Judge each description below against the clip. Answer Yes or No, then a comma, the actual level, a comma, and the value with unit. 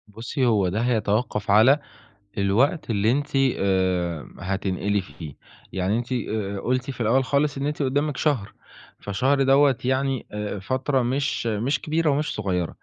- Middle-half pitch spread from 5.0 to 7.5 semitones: Yes, wide, 5.4 semitones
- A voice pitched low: Yes, low, 120 Hz